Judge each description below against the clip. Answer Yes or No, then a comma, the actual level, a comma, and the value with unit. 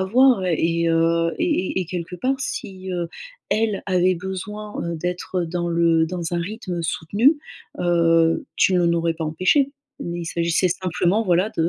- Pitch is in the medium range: Yes, medium, 175 Hz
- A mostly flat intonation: Yes, narrow, 2.2 semitones